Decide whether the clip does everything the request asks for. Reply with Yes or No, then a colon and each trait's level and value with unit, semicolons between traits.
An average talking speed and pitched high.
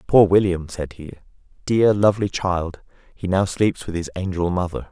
No: average, 170 wpm; very low, 95 Hz